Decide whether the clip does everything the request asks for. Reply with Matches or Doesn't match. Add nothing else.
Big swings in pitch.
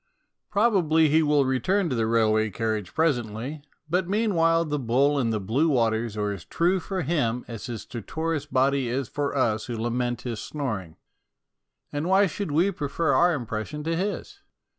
Matches